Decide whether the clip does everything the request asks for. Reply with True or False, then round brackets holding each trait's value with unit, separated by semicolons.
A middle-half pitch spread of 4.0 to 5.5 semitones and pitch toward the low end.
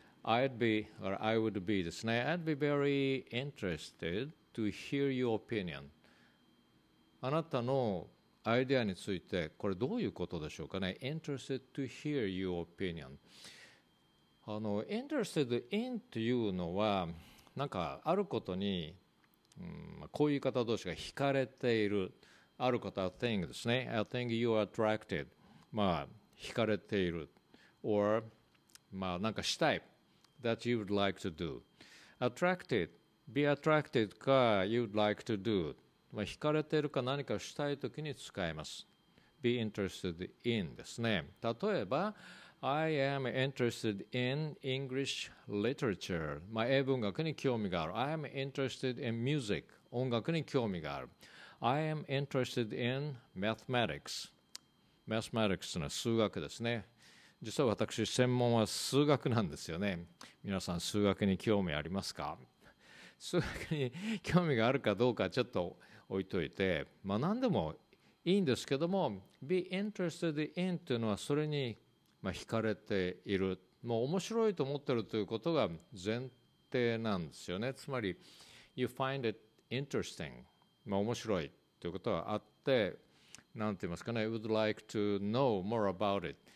True (5.1 semitones; 115 Hz)